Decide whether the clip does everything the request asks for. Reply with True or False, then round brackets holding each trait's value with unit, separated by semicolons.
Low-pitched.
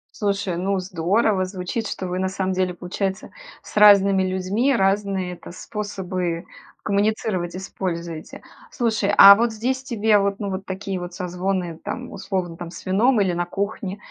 False (190 Hz)